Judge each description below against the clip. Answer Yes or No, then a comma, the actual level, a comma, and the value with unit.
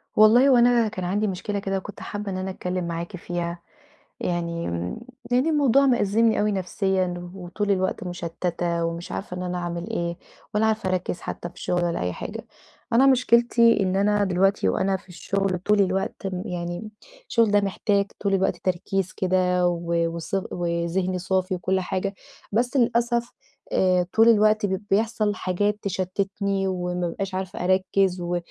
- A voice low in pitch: No, high, 190 Hz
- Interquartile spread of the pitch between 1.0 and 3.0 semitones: Yes, average, 2.7 semitones